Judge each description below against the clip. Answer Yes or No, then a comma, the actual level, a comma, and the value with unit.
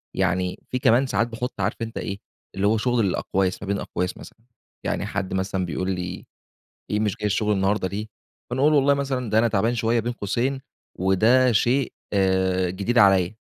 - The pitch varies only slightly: No, average, 4.0 semitones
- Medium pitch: No, low, 105 Hz